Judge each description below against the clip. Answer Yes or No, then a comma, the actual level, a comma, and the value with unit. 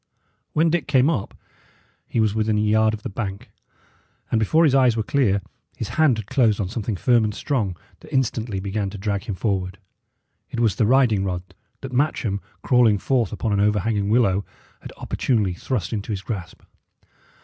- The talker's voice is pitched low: Yes, low, 110 Hz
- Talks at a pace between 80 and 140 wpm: No, average, 180 wpm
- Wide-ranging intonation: No, average, 3.7 semitones